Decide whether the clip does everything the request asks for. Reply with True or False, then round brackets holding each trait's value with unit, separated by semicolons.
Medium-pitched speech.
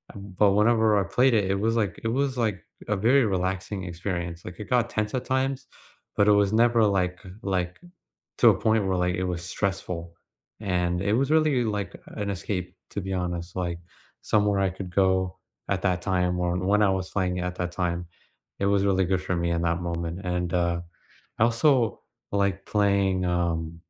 False (95 Hz)